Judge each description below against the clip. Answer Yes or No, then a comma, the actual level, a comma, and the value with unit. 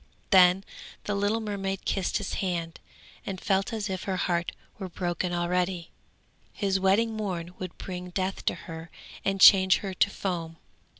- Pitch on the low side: No, high, 190 Hz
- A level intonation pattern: Yes, narrow, 1.8 semitones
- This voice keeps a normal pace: Yes, average, 160 wpm